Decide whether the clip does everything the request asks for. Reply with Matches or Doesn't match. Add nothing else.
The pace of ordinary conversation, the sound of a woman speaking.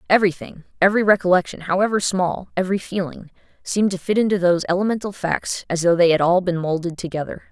Matches